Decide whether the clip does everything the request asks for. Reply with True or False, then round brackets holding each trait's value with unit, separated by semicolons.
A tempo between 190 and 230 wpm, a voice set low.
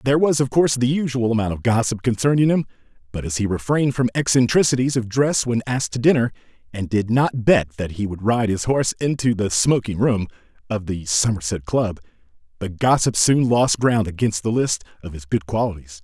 True (200 wpm; 115 Hz)